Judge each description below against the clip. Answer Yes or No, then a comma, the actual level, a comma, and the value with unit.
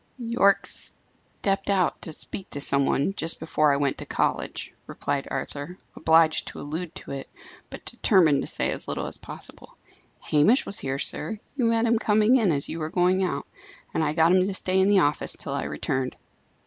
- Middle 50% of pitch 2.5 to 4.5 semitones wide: No, wide, 5.4 semitones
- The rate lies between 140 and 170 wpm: No, average, 200 wpm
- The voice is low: No, medium, 175 Hz